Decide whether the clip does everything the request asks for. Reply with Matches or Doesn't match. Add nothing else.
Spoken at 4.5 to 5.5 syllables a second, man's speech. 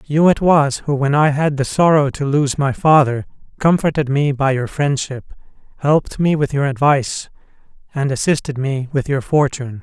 Matches